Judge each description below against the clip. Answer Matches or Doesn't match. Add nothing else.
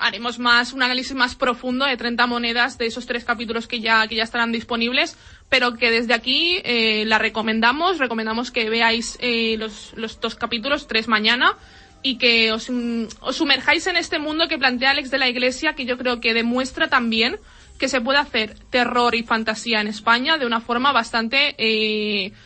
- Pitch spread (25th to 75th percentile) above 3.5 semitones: Doesn't match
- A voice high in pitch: Matches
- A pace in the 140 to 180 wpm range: Doesn't match